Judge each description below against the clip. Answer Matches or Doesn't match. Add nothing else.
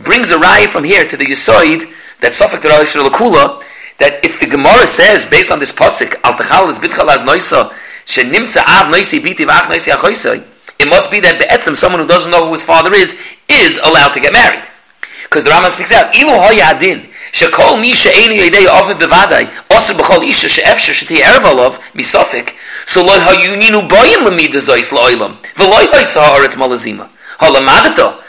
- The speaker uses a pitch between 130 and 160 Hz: Doesn't match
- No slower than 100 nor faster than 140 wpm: Doesn't match